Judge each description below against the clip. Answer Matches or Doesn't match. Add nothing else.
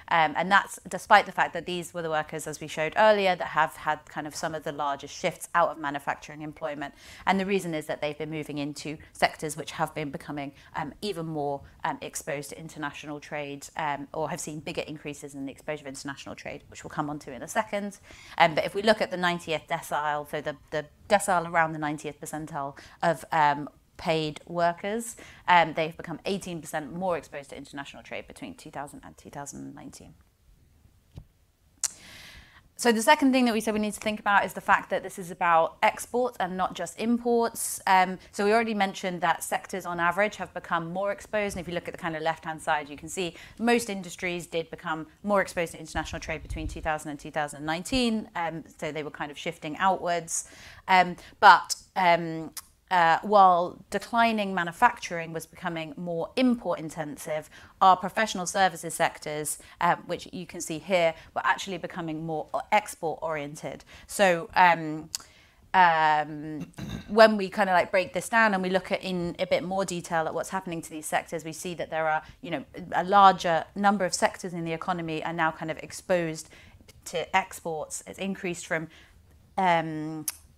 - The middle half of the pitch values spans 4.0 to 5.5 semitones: Doesn't match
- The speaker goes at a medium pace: Matches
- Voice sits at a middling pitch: Matches